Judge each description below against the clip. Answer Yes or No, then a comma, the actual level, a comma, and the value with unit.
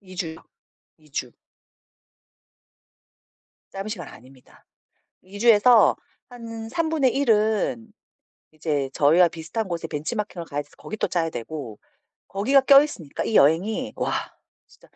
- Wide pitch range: Yes, wide, 6.5 semitones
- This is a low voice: No, high, 190 Hz